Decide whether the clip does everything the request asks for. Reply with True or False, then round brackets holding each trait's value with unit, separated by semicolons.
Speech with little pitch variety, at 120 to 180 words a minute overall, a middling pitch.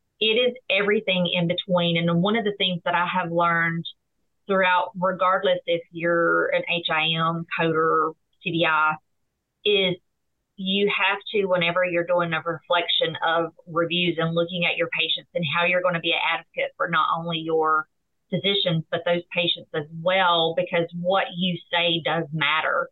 True (1.6 semitones; 160 wpm; 175 Hz)